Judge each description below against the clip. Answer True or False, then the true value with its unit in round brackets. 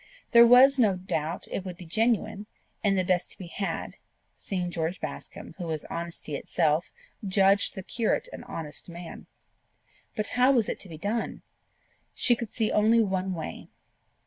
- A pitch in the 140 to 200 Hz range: True (190 Hz)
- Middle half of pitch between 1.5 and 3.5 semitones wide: False (4.4 semitones)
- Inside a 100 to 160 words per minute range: False (170 wpm)